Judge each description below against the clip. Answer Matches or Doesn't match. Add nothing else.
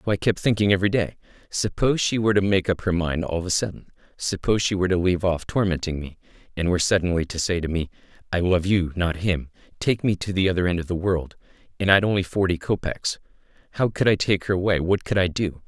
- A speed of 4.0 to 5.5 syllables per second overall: Doesn't match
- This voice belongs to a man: Matches